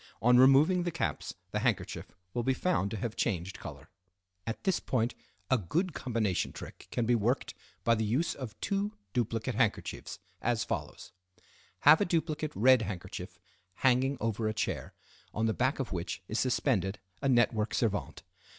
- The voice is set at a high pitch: No, low, 120 Hz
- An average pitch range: Yes, average, 3.9 semitones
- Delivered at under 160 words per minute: No, average, 165 wpm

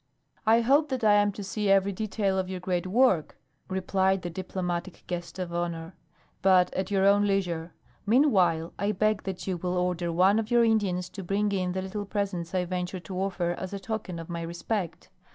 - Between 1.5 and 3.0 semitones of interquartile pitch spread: Yes, narrow, 2.4 semitones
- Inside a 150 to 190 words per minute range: No, average, 200 wpm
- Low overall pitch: No, high, 190 Hz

